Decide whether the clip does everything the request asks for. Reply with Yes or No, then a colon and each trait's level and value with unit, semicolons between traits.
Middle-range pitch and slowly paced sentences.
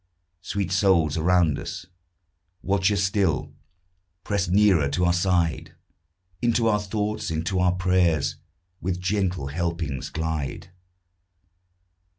No: very low, 90 Hz; slow, 110 wpm